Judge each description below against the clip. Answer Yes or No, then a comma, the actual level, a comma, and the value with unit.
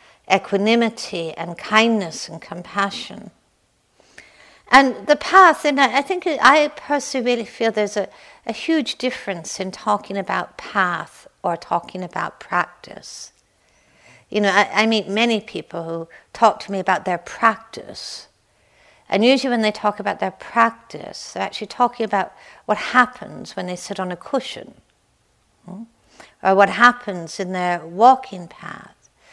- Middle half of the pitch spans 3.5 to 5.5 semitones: Yes, average, 4.2 semitones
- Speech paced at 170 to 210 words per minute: No, average, 140 wpm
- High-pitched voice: Yes, high, 210 Hz